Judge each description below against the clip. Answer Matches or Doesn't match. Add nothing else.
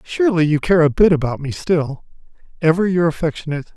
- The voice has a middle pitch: Matches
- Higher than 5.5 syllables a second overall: Matches